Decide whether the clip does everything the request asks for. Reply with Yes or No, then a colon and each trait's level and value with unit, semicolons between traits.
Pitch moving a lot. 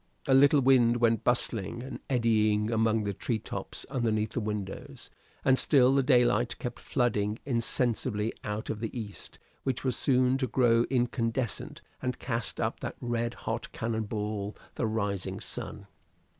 No: average, 2.7 semitones